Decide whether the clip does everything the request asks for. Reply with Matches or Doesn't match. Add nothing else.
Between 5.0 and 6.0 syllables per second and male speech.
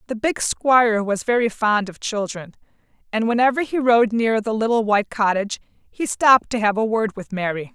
Doesn't match